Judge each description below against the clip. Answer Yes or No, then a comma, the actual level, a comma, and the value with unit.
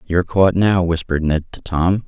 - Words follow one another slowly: No, average, 200 wpm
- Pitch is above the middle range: No, very low, 90 Hz